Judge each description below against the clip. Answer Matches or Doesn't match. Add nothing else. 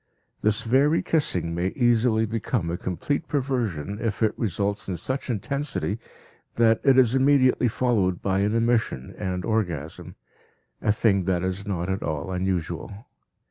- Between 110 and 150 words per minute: Matches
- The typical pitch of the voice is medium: Doesn't match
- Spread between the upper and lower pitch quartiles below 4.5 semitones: Doesn't match